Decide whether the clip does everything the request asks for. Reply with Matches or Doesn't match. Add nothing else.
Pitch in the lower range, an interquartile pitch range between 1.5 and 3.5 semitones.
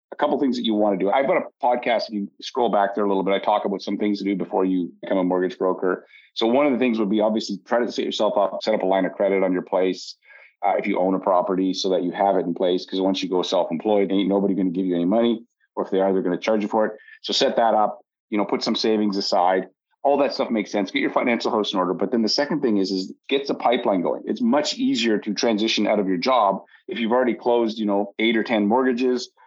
Matches